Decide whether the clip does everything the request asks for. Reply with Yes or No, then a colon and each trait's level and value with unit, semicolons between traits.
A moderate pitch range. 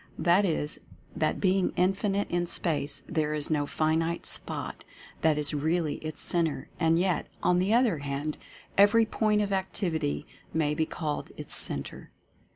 Yes: average, 3.9 semitones